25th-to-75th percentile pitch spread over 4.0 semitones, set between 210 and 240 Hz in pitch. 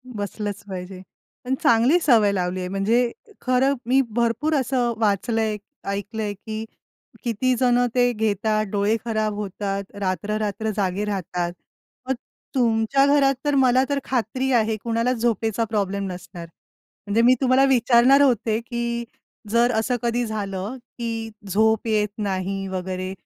No: average, 3.3 semitones; high, 220 Hz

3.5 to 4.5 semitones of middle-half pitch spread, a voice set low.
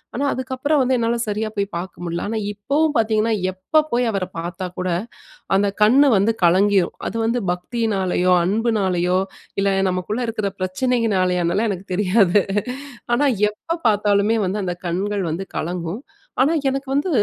No: average, 4.2 semitones; high, 205 Hz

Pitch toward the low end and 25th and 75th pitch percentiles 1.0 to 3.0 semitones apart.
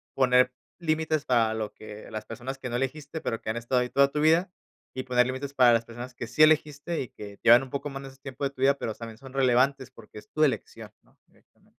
Yes: low, 130 Hz; average, 2.7 semitones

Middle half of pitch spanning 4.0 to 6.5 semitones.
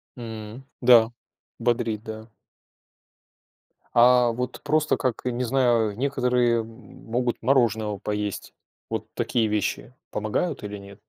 No: narrow, 2.6 semitones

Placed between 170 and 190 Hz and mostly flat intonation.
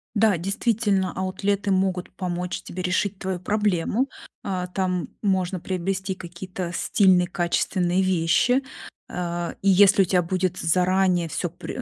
Yes: medium, 185 Hz; narrow, 1.6 semitones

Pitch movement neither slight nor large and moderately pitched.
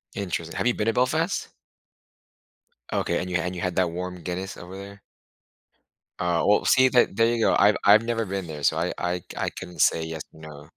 No: average, 3.7 semitones; very low, 90 Hz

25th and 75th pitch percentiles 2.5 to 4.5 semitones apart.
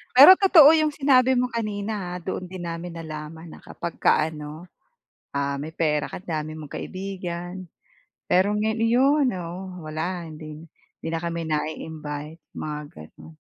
No: average, 4.9 semitones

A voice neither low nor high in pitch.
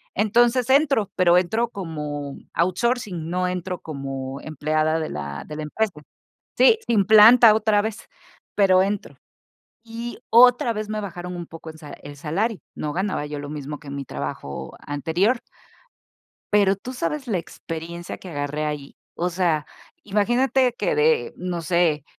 Yes: medium, 180 Hz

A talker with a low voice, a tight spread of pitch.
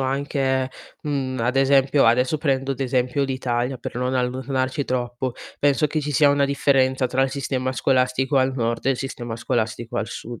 Yes: low, 130 Hz; narrow, 1.6 semitones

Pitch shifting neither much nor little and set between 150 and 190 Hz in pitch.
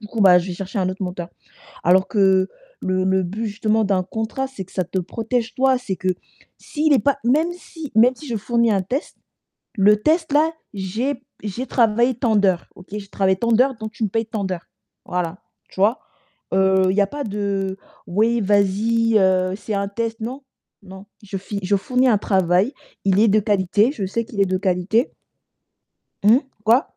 No: average, 3.6 semitones; high, 205 Hz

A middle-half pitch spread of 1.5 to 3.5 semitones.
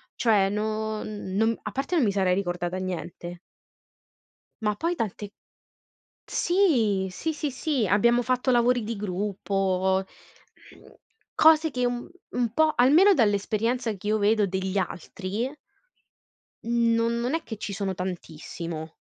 No: average, 4.3 semitones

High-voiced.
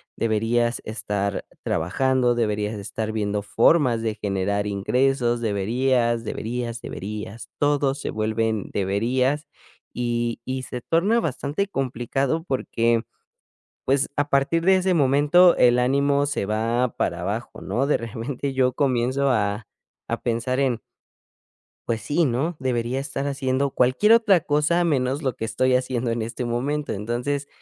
No: low, 125 Hz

